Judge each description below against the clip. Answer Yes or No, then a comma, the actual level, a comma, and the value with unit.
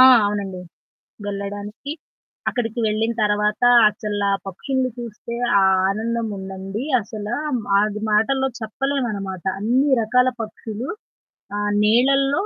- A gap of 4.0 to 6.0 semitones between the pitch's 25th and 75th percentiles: No, average, 3.2 semitones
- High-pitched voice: Yes, high, 215 Hz